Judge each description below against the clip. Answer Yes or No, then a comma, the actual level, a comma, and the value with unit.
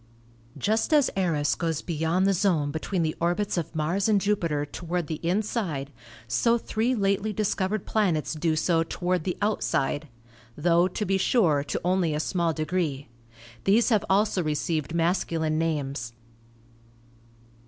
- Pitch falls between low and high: Yes, medium, 175 Hz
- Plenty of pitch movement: No, average, 4.1 semitones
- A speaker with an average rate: Yes, average, 150 wpm